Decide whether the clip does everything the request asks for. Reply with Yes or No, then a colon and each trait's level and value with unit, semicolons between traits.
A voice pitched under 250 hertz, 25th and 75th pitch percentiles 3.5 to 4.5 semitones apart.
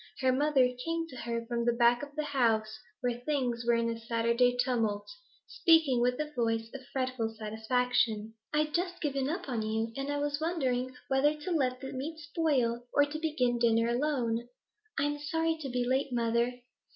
No: very high, 255 Hz; average, 3.8 semitones